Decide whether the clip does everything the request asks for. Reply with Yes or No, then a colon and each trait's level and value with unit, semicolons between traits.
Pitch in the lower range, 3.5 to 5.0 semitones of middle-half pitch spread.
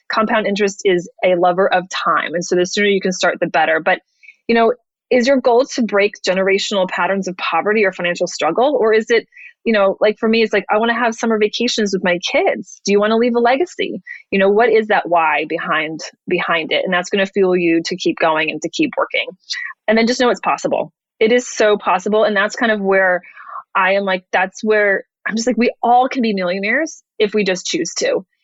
No: high, 210 Hz; average, 4.0 semitones